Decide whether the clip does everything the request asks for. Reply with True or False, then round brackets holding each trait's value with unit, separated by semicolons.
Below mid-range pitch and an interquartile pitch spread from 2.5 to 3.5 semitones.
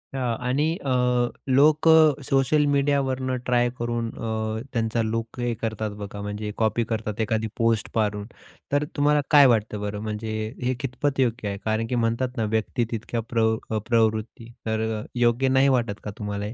True (115 Hz; 2.9 semitones)